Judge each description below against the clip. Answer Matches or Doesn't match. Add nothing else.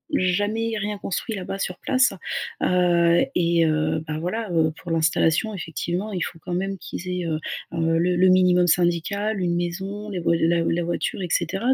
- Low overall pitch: Doesn't match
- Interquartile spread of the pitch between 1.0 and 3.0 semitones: Matches